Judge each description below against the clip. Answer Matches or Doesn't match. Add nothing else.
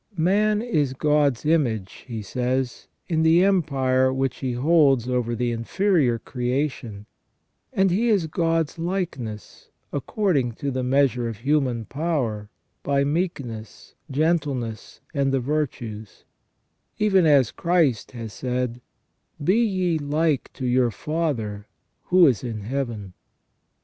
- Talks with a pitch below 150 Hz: Matches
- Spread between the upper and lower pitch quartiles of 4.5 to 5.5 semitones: Matches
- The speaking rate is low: Matches